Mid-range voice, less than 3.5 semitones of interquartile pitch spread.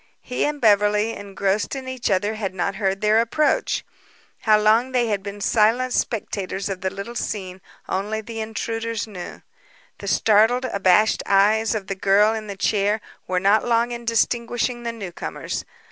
No: high, 215 Hz; narrow, 2.6 semitones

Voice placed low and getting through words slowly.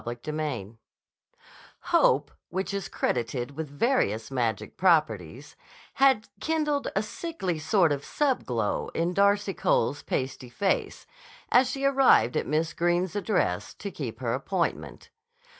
No: medium, 160 Hz; slow, 130 wpm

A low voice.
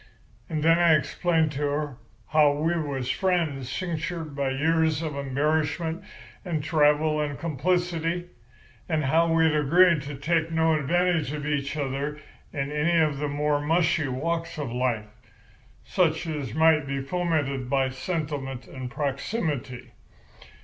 No: medium, 150 Hz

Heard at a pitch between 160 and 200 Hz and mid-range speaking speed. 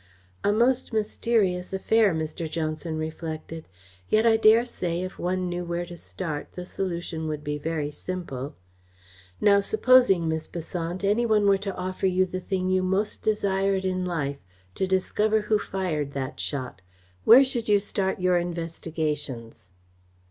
Yes: medium, 185 Hz; average, 155 wpm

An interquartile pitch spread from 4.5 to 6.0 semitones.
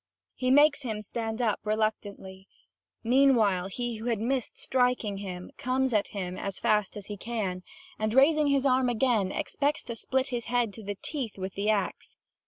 No: average, 4.1 semitones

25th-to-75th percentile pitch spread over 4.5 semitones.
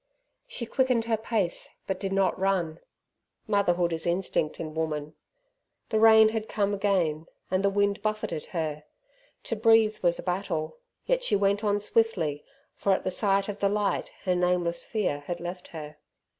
No: average, 3.8 semitones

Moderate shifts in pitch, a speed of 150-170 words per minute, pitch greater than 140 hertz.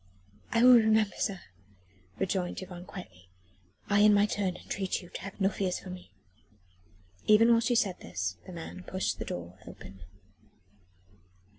Yes: average, 3.0 semitones; average, 155 wpm; high, 190 Hz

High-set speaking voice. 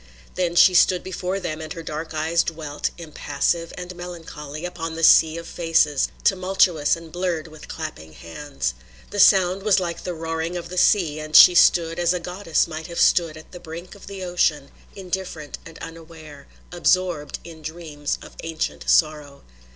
No: medium, 165 Hz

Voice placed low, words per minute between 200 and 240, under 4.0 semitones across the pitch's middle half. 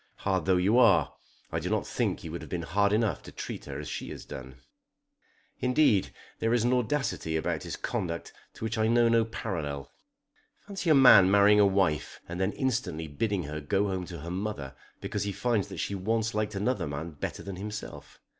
No: low, 100 Hz; fast, 205 wpm; average, 5.0 semitones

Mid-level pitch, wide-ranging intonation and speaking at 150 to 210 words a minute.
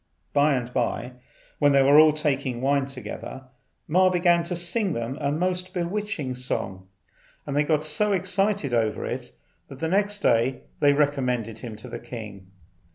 Yes: medium, 145 Hz; wide, 5.7 semitones; average, 160 wpm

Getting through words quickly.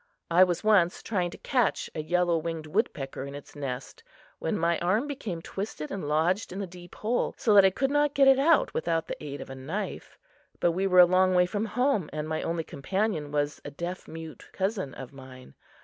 Yes: fast, 215 wpm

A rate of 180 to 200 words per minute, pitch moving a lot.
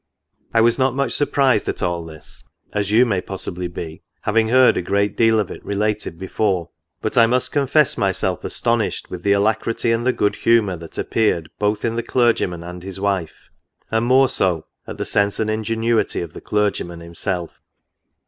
No: average, 185 wpm; average, 4.1 semitones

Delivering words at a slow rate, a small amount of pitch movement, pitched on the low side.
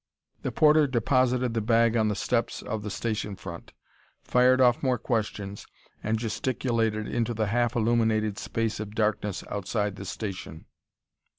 No: average, 150 wpm; narrow, 2.2 semitones; low, 110 Hz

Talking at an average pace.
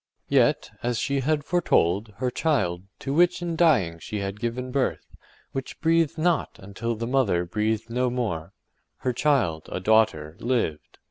Yes: average, 155 wpm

